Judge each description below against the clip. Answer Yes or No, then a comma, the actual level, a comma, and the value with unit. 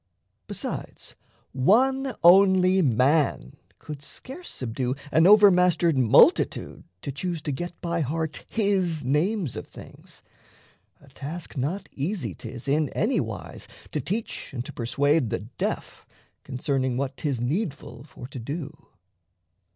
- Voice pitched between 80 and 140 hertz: No, medium, 155 Hz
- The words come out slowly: Yes, slow, 130 wpm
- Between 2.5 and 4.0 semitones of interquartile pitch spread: No, wide, 5.5 semitones